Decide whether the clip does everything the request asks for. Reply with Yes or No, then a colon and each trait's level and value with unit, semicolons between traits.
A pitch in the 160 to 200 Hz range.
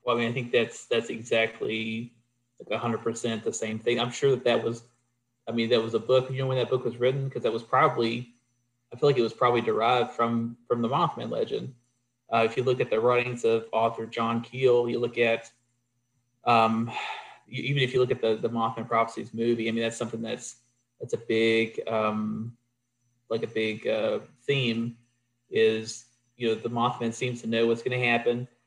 No: low, 120 Hz